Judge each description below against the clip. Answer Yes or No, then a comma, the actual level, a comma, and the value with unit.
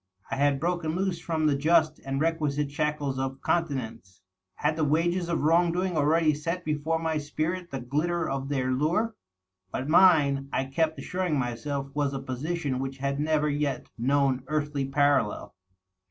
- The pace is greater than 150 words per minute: Yes, average, 165 wpm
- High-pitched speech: No, medium, 150 Hz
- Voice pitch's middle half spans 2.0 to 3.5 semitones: Yes, average, 3.1 semitones